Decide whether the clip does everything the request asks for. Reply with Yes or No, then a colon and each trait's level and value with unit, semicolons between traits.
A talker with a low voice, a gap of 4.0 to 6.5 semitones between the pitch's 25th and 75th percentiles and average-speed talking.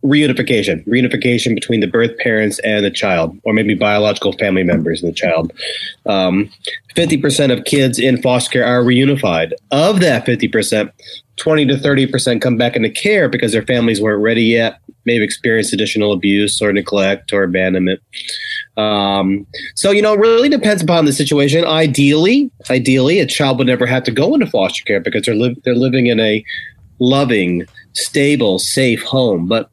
Yes: low, 125 Hz; average, 5.1 semitones; average, 180 wpm